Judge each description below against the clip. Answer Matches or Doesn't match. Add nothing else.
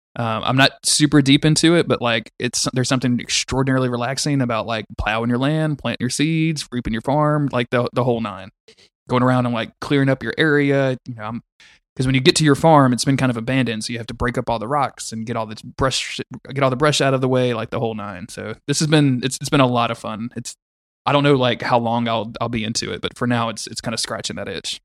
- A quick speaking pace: Matches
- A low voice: Matches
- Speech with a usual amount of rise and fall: Matches